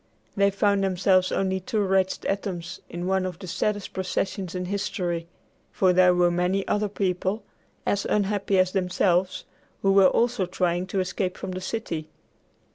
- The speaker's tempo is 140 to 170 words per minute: Yes, average, 160 wpm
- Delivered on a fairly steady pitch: Yes, narrow, 1.6 semitones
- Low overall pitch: No, high, 190 Hz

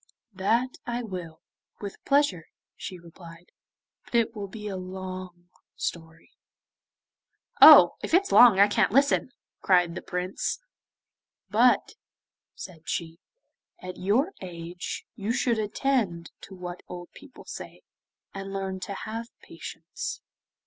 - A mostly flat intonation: No, average, 4.4 semitones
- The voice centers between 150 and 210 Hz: Yes, high, 190 Hz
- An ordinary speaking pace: No, slow, 125 wpm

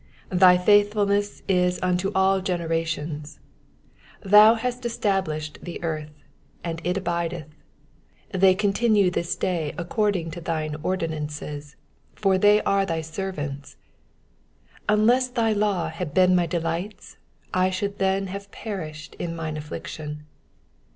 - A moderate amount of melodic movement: Yes, average, 3.7 semitones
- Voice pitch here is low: No, medium, 180 Hz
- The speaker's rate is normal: No, slow, 130 wpm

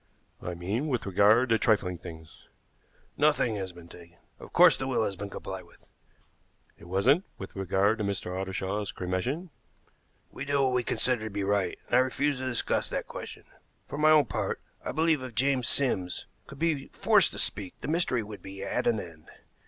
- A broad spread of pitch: Yes, wide, 5.7 semitones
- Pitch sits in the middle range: No, low, 105 Hz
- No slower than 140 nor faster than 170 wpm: No, average, 190 wpm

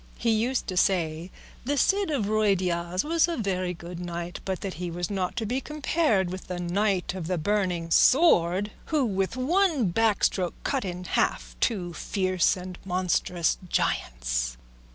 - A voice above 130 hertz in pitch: Yes, medium, 185 Hz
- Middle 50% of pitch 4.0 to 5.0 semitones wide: Yes, average, 4.3 semitones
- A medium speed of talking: Yes, average, 165 wpm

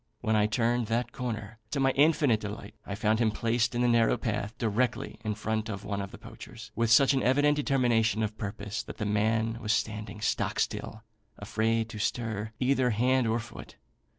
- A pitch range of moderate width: No, narrow, 2.2 semitones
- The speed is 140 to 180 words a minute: No, average, 195 wpm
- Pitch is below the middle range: Yes, low, 115 Hz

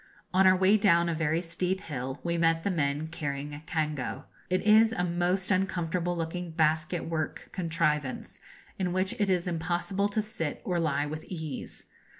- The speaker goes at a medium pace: Yes, average, 170 wpm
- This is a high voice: No, medium, 170 Hz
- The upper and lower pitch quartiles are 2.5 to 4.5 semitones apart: Yes, average, 2.8 semitones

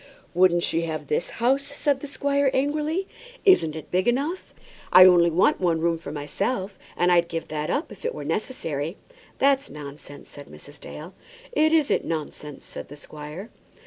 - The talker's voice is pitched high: No, medium, 180 Hz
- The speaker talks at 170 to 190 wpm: Yes, average, 175 wpm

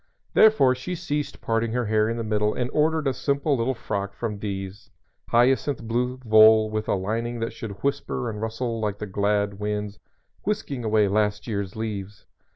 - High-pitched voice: No, low, 110 Hz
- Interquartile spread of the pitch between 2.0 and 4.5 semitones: Yes, average, 3.0 semitones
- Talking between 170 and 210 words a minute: Yes, average, 180 wpm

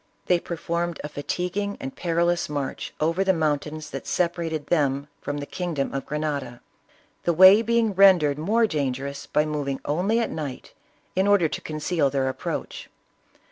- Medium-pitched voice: Yes, medium, 155 Hz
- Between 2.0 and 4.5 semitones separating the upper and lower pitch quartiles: Yes, average, 3.9 semitones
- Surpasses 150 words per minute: Yes, average, 165 wpm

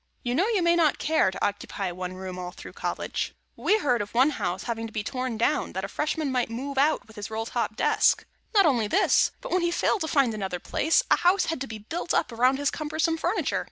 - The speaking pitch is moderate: No, very high, 255 Hz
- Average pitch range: No, wide, 6.9 semitones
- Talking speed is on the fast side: Yes, fast, 245 wpm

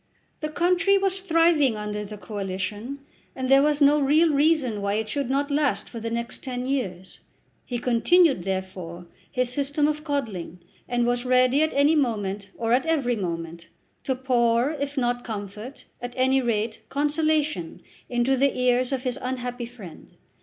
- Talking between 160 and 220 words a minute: Yes, average, 165 wpm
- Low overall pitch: No, very high, 250 Hz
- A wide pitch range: No, average, 4.7 semitones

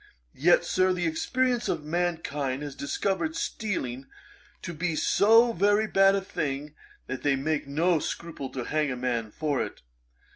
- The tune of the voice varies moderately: Yes, average, 5.0 semitones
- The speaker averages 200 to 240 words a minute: No, average, 155 wpm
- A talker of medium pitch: Yes, medium, 160 Hz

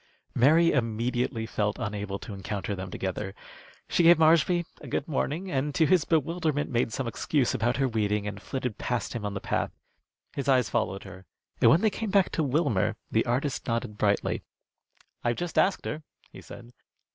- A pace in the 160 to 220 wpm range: Yes, average, 180 wpm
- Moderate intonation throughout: No, wide, 6.9 semitones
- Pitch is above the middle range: No, low, 125 Hz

